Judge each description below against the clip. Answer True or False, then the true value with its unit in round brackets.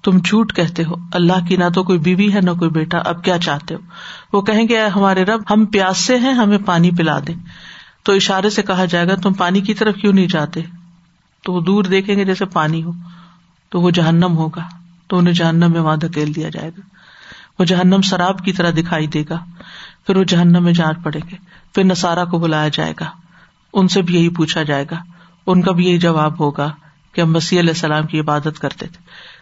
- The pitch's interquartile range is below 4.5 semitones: True (2.5 semitones)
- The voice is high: False (175 Hz)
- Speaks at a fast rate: True (220 wpm)